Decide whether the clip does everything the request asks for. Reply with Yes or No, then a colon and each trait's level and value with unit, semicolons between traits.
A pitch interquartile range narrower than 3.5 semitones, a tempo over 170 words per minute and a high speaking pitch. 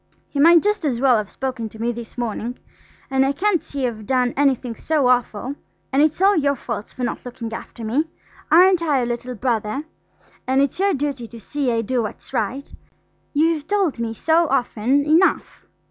No: average, 4.2 semitones; average, 190 wpm; very high, 265 Hz